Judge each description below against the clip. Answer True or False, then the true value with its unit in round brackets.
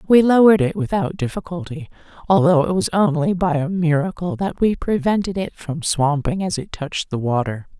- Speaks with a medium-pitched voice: True (170 Hz)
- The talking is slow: False (175 wpm)